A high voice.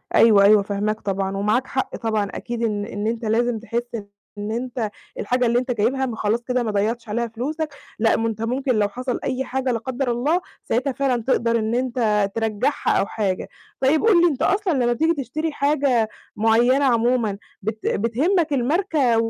Yes: high, 235 Hz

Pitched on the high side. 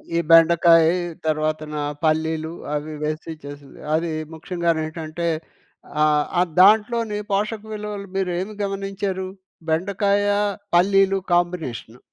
No: medium, 170 Hz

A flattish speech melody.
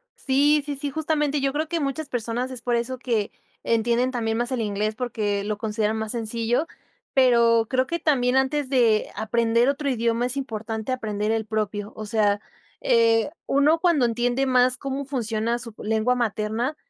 No: average, 3.3 semitones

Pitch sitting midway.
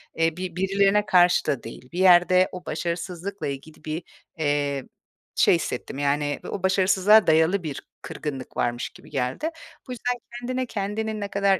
Yes: medium, 180 Hz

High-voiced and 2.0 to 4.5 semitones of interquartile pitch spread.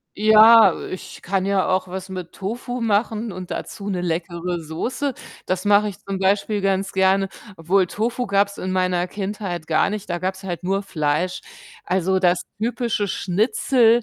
Yes: high, 195 Hz; narrow, 2.5 semitones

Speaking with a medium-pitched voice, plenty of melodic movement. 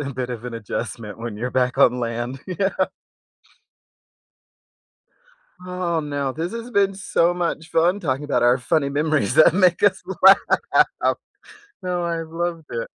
Yes: medium, 155 Hz; wide, 6.1 semitones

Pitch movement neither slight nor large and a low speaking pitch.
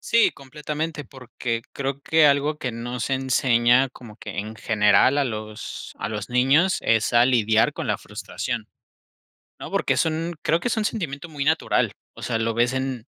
Yes: average, 4.3 semitones; low, 130 Hz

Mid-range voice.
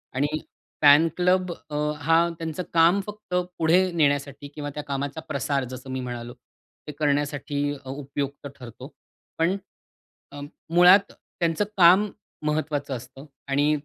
Yes: medium, 145 Hz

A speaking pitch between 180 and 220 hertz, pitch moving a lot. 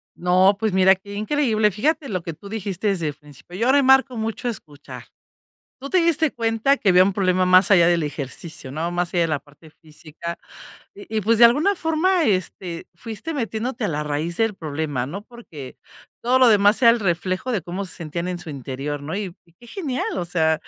Yes: high, 190 Hz; wide, 5.7 semitones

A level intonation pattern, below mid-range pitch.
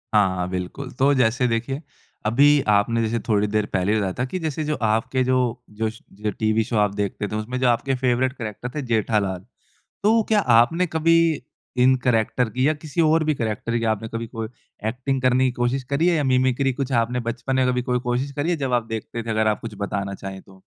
No: average, 3.7 semitones; low, 120 Hz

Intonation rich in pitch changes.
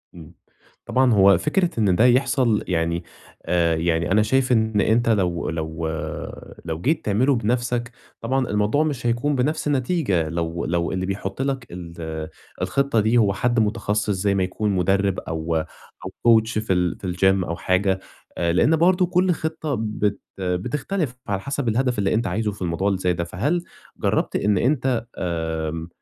Yes: wide, 5.9 semitones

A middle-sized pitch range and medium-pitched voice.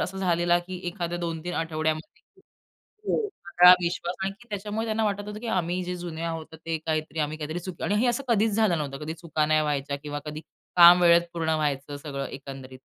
Yes: average, 3.0 semitones; medium, 170 Hz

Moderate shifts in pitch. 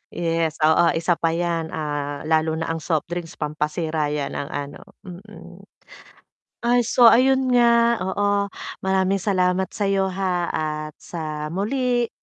Yes: average, 4.0 semitones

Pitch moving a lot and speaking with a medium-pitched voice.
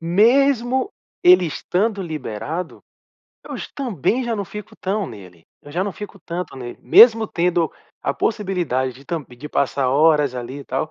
Yes: wide, 7.0 semitones; medium, 175 Hz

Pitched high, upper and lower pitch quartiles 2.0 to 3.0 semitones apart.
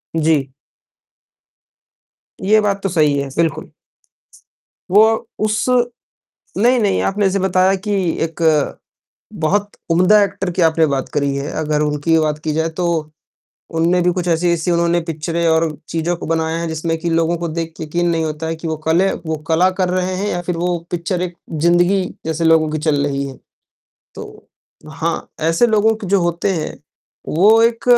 No: medium, 170 Hz; average, 2.7 semitones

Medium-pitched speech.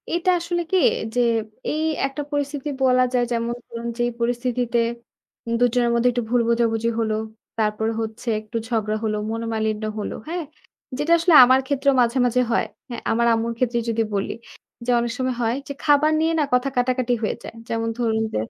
No: high, 240 Hz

